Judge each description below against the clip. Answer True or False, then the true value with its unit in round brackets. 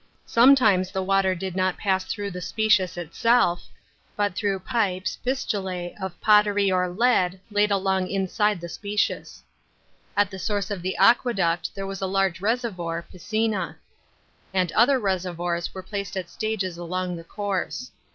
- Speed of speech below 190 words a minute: True (150 wpm)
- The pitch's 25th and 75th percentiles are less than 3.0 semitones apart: True (2.4 semitones)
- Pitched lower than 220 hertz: True (190 Hz)